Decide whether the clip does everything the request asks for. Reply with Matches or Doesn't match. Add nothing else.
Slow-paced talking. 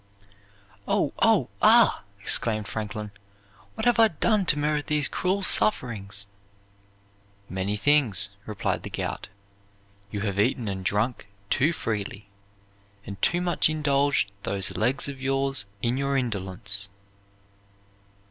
Matches